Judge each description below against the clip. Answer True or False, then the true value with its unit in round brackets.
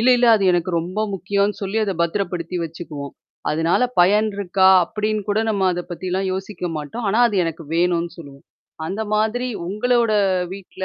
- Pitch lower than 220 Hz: True (190 Hz)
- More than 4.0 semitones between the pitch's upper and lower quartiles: False (3.6 semitones)